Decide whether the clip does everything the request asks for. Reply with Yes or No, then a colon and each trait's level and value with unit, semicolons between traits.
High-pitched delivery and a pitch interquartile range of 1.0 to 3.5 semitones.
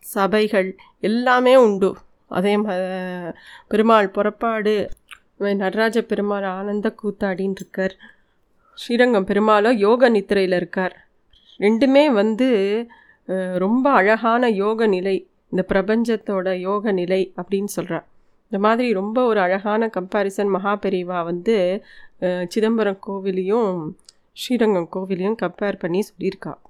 Yes: high, 200 Hz; narrow, 2.6 semitones